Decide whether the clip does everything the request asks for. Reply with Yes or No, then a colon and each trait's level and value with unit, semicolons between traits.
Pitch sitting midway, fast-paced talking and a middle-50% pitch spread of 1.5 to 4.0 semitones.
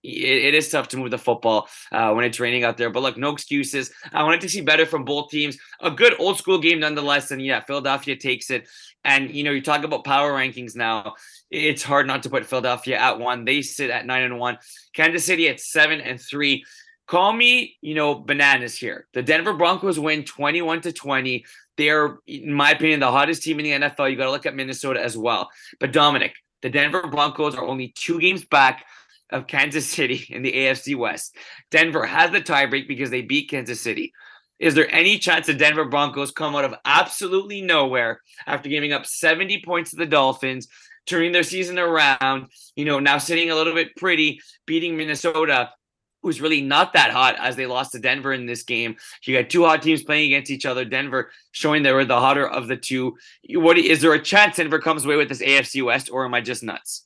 Yes: medium, 145 Hz; fast, 215 wpm; average, 3.3 semitones